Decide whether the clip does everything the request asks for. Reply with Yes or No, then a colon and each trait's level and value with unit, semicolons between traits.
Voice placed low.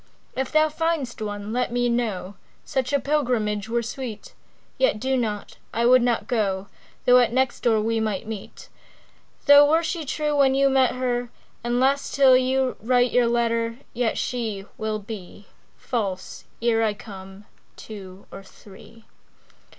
No: high, 240 Hz